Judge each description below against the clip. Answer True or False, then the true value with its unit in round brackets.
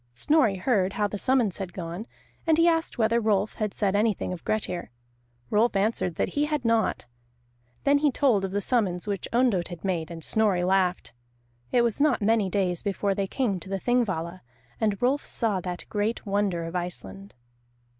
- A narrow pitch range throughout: False (4.0 semitones)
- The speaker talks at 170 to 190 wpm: True (185 wpm)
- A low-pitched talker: False (205 Hz)